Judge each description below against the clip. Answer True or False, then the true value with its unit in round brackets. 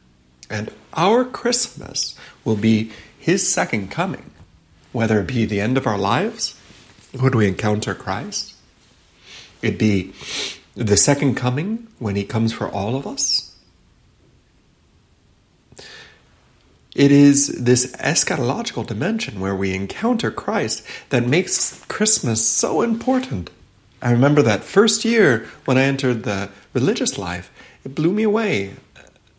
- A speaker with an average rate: False (125 wpm)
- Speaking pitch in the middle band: False (110 Hz)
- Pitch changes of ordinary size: False (6.3 semitones)